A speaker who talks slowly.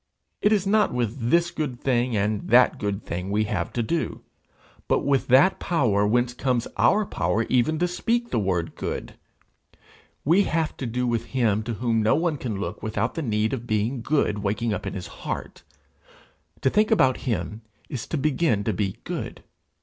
No: average, 190 wpm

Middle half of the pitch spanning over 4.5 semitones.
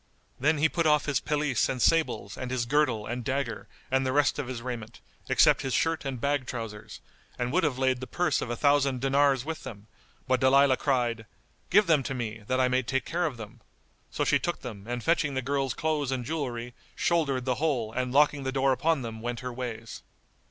No: average, 3.0 semitones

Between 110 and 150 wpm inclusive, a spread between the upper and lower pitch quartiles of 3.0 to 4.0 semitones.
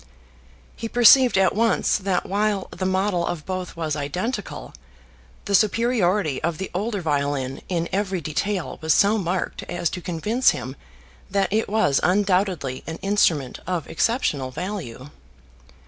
No: average, 140 wpm; average, 4.6 semitones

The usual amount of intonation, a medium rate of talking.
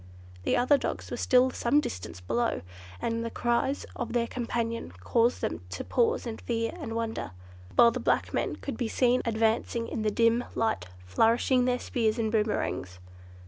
No: narrow, 1.6 semitones; average, 175 wpm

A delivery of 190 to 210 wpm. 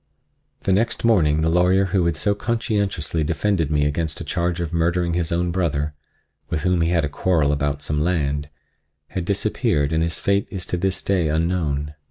No: average, 180 wpm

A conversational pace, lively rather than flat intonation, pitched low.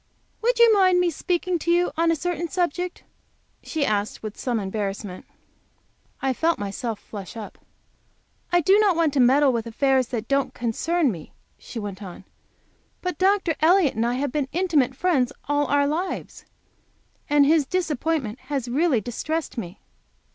No: average, 160 wpm; wide, 6.6 semitones; very high, 285 Hz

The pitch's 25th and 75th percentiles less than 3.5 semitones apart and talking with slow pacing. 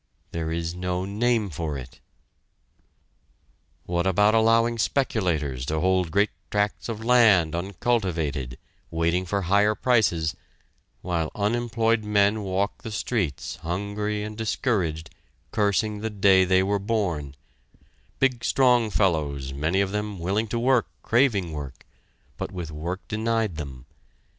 No: average, 4.7 semitones; slow, 130 wpm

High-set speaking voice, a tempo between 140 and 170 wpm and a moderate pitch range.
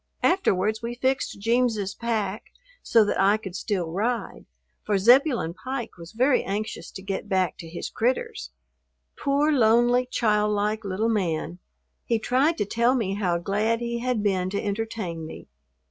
Yes: high, 215 Hz; average, 155 wpm; average, 3.7 semitones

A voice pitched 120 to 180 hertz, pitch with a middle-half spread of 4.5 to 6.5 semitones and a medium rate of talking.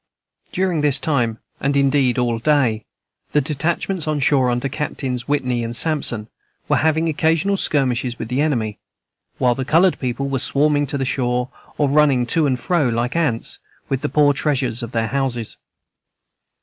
No: low, 135 Hz; average, 3.5 semitones; average, 165 wpm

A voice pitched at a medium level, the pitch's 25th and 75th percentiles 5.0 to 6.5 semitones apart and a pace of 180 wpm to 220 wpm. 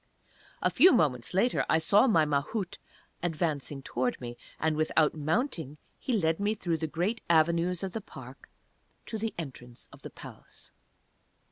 No: medium, 160 Hz; average, 5.3 semitones; average, 155 wpm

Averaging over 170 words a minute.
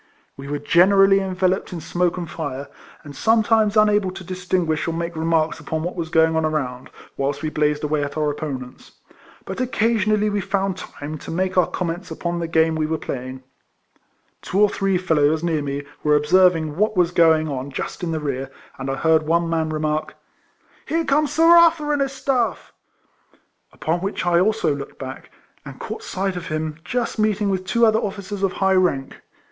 Yes: average, 195 wpm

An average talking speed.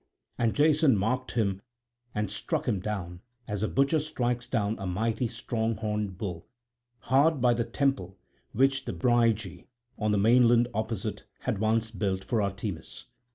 Yes: average, 155 wpm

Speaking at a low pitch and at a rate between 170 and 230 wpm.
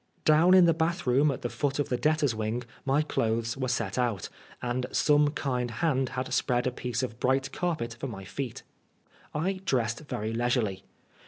Yes: low, 130 Hz; average, 180 wpm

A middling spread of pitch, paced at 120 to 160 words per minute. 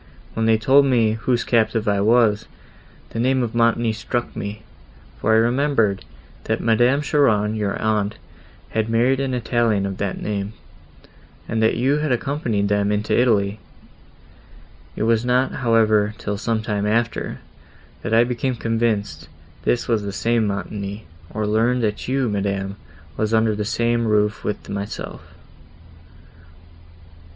No: narrow, 2.3 semitones; average, 145 wpm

